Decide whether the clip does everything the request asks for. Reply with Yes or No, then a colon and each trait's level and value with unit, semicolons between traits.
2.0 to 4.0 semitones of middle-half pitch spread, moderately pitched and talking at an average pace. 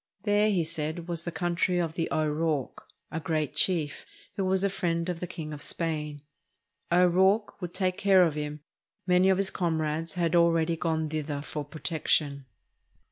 Yes: average, 2.7 semitones; medium, 165 Hz; average, 170 wpm